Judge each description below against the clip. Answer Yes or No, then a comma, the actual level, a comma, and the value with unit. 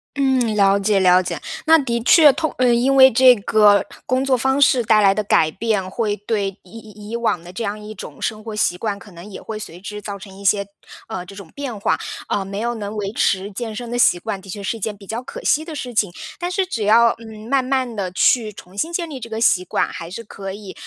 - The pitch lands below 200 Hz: No, high, 215 Hz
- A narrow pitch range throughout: No, average, 3.5 semitones